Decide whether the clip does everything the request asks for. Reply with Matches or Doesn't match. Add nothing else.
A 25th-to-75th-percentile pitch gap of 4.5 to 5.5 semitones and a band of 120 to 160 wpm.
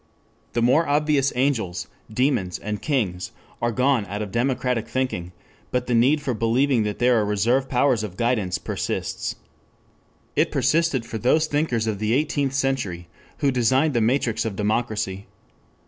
Doesn't match